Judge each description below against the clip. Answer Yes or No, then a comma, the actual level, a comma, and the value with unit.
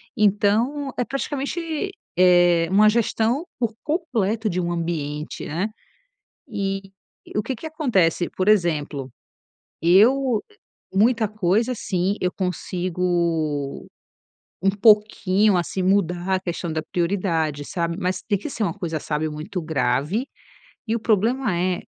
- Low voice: No, high, 190 Hz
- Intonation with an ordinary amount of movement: Yes, average, 4.4 semitones